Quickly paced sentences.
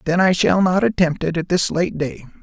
Yes: fast, 245 wpm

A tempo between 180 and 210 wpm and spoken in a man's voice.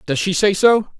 No: fast, 240 wpm; male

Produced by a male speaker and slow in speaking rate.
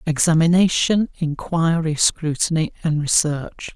Yes: male; slow, 80 wpm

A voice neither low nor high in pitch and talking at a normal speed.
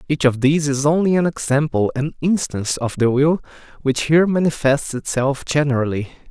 Yes: medium, 145 Hz; average, 160 wpm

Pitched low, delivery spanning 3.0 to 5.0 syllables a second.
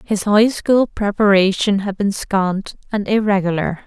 No: high, 200 Hz; 4.2 syllables/s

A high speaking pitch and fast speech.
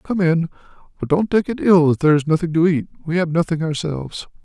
No: medium, 160 Hz; fast, 230 wpm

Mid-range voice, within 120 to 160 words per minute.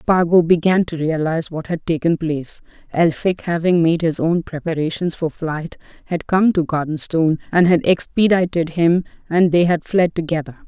Yes: medium, 165 Hz; average, 155 wpm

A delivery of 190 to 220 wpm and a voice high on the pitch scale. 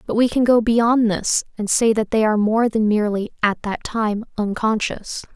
Yes: average, 200 wpm; high, 220 Hz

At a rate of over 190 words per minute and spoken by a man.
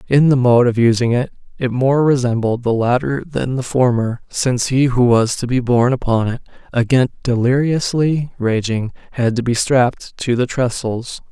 No: average, 175 wpm; male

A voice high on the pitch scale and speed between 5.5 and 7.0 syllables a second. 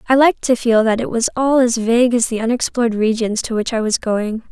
Yes: high, 235 Hz; 5.9 syllables/s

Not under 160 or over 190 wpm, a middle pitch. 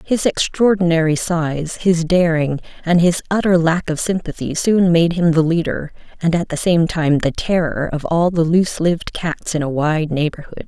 Yes: average, 175 wpm; medium, 165 Hz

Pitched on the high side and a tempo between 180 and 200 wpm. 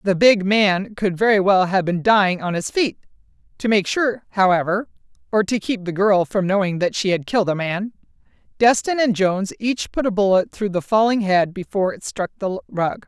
Yes: high, 200 Hz; average, 195 wpm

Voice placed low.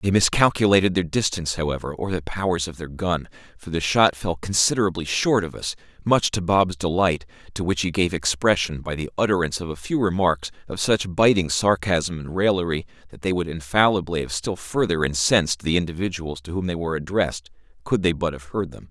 Yes: very low, 90 Hz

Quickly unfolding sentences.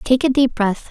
Yes: fast, 265 wpm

